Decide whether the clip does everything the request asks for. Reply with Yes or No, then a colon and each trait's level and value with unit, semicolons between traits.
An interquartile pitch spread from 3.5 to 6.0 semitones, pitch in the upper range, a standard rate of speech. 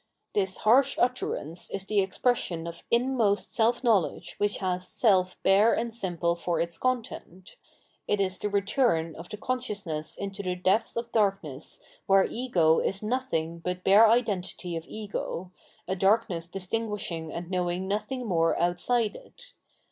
Yes: average, 4.4 semitones; high, 195 Hz; average, 150 wpm